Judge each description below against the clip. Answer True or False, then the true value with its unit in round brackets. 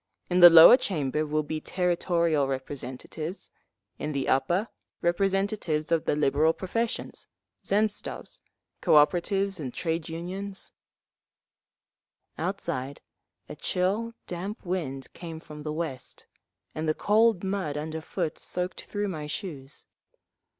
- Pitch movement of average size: True (4.2 semitones)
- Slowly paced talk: True (110 wpm)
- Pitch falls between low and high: True (165 Hz)